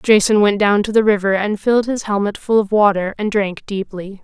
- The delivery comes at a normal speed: No, fast, 225 wpm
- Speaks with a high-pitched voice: Yes, high, 205 Hz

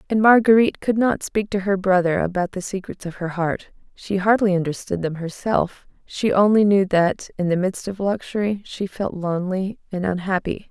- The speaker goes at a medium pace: Yes, average, 185 wpm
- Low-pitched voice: No, high, 190 Hz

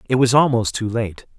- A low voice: Yes, low, 115 Hz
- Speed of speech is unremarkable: No, fast, 215 wpm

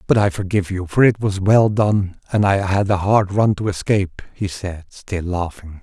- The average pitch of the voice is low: Yes, very low, 95 Hz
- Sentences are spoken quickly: Yes, fast, 215 wpm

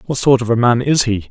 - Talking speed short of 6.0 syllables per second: No, 6.1 syllables/s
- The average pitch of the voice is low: Yes, low, 120 Hz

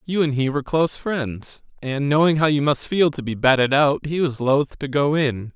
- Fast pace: Yes, fast, 240 wpm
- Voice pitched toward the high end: No, medium, 145 Hz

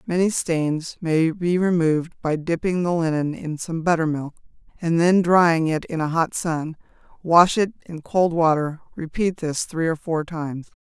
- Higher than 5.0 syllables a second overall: No, 4.4 syllables/s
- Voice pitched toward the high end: No, medium, 165 Hz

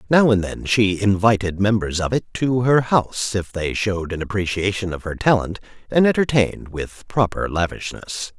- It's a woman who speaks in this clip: No, male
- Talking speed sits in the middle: Yes, average, 170 wpm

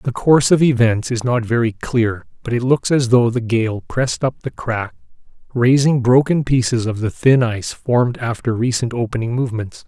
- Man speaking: Yes, male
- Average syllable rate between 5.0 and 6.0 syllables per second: Yes, 5.1 syllables/s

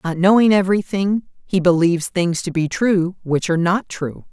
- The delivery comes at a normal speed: Yes, average, 180 wpm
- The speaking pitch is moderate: Yes, medium, 180 Hz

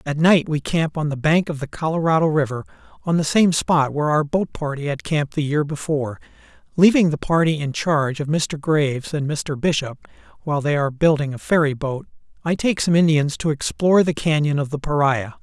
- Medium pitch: Yes, medium, 150 Hz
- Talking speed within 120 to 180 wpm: No, average, 200 wpm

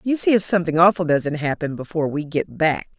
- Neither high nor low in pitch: Yes, medium, 165 Hz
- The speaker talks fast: Yes, fast, 220 wpm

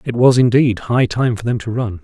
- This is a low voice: Yes, low, 115 Hz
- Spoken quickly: Yes, fast, 265 wpm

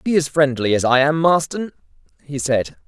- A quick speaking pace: No, average, 190 wpm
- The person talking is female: No, male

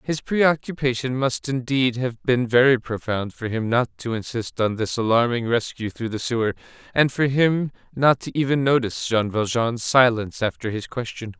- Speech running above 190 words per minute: No, average, 175 wpm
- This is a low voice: Yes, low, 125 Hz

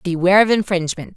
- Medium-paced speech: Yes, average, 155 wpm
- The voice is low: No, medium, 185 Hz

